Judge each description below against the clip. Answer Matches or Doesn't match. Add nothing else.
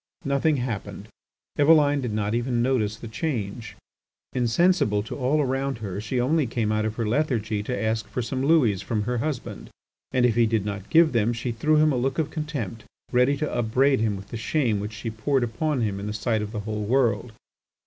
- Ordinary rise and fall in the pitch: Matches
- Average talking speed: Doesn't match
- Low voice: Matches